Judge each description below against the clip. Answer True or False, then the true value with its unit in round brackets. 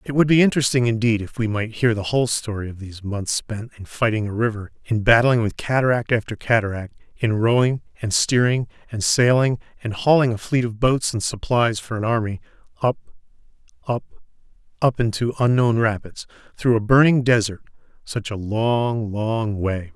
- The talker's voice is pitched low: True (115 Hz)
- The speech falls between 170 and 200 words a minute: True (175 wpm)